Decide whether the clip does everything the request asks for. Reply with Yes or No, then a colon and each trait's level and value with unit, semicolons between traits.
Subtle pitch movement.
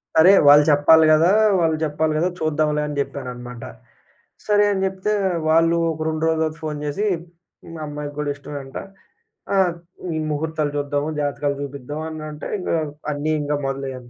Yes: narrow, 1.9 semitones